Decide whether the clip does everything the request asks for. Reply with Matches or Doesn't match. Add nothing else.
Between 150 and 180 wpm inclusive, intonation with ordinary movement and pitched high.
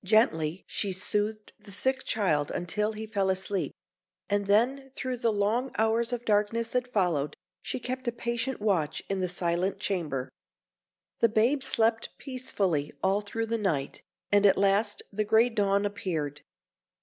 Matches